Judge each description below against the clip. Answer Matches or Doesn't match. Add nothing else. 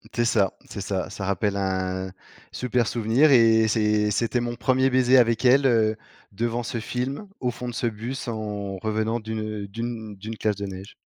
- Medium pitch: Doesn't match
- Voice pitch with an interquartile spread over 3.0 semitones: Doesn't match